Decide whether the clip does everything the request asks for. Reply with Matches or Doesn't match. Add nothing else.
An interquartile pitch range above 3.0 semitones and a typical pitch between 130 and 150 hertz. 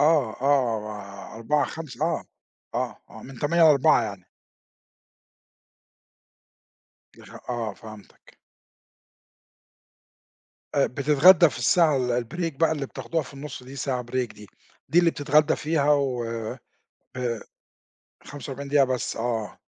Matches